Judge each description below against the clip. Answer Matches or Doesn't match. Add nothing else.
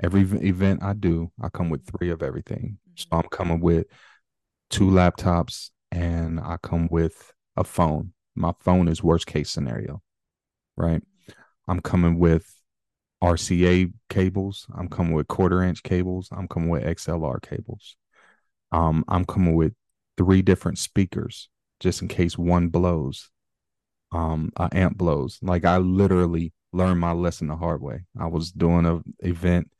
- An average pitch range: Doesn't match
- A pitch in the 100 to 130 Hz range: Doesn't match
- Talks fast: Doesn't match